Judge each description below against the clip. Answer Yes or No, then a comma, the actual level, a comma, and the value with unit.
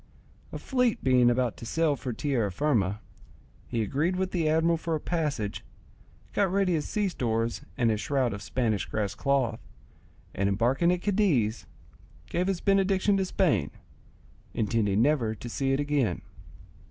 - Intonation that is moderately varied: No, wide, 7.4 semitones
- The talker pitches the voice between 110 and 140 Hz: Yes, low, 135 Hz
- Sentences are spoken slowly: No, average, 155 wpm